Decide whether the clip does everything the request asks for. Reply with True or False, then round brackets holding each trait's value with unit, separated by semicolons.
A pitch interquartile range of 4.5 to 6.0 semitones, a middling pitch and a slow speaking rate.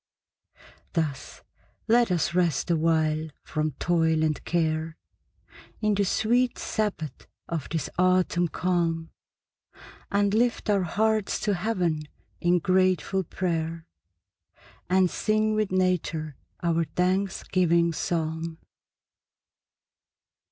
False (3.1 semitones; 175 Hz; 95 wpm)